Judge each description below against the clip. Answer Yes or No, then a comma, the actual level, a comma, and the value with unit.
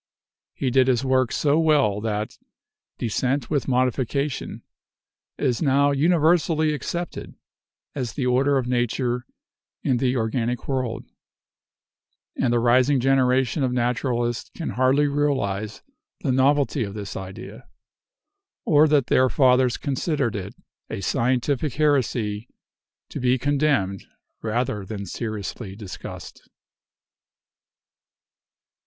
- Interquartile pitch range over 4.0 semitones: No, average, 3.2 semitones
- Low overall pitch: Yes, low, 130 Hz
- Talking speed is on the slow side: Yes, slow, 110 wpm